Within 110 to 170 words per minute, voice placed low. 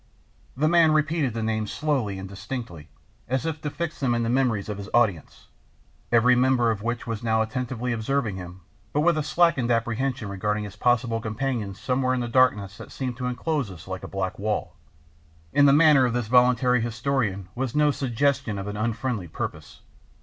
No: average, 190 wpm; low, 120 Hz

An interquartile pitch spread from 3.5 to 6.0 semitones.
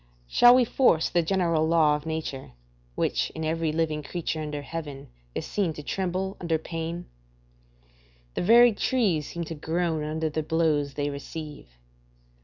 No: narrow, 2.4 semitones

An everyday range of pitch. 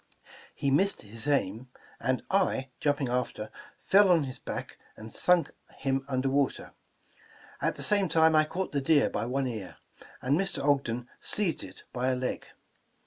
Yes: average, 4.3 semitones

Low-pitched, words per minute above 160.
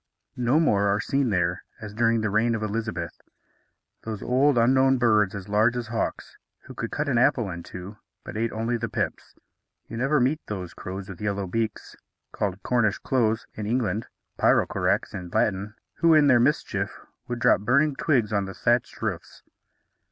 Yes: low, 110 Hz; average, 175 wpm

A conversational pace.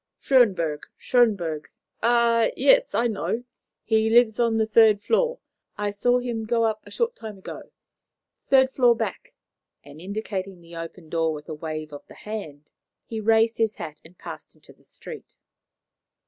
Yes: average, 160 wpm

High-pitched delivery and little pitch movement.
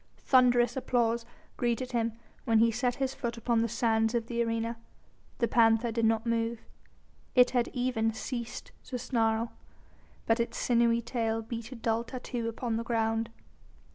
Yes: high, 230 Hz; narrow, 1.3 semitones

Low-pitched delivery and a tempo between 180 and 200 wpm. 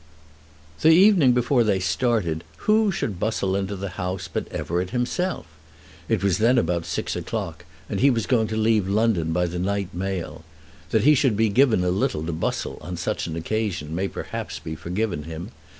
Yes: low, 100 Hz; average, 185 wpm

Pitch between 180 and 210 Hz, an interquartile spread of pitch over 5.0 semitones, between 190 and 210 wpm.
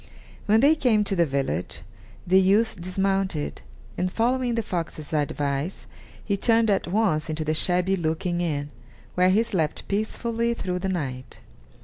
No: medium, 185 Hz; wide, 5.4 semitones; average, 150 wpm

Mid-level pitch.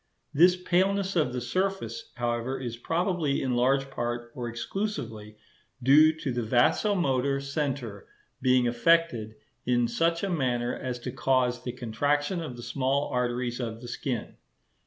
No: low, 130 Hz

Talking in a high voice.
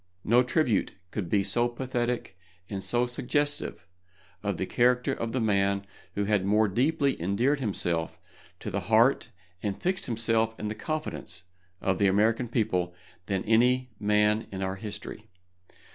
No: low, 110 Hz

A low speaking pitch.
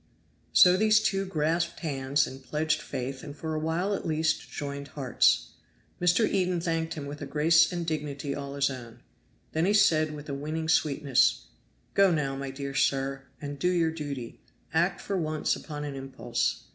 No: medium, 155 Hz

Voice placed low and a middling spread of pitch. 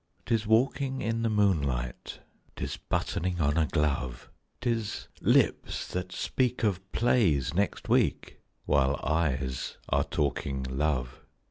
No: very low, 80 Hz; wide, 8.0 semitones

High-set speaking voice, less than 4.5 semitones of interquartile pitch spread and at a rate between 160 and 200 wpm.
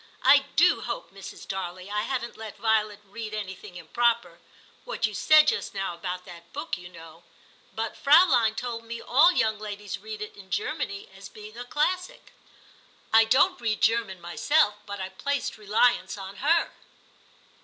Yes: high, 215 Hz; average, 4.0 semitones; average, 175 wpm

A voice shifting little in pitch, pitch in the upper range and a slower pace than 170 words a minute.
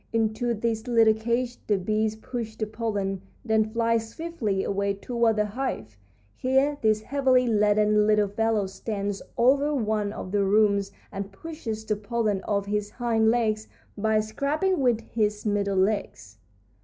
Yes: narrow, 2.3 semitones; high, 220 Hz; average, 150 wpm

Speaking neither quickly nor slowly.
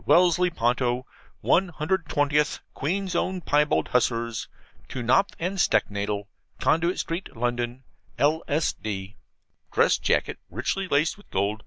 No: slow, 120 wpm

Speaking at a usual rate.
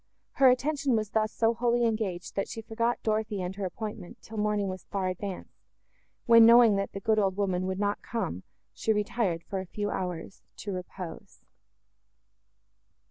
Yes: average, 170 wpm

